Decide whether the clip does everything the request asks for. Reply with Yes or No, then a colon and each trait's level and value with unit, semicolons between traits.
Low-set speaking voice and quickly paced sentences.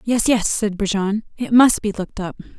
No: high, 210 Hz; fast, 210 wpm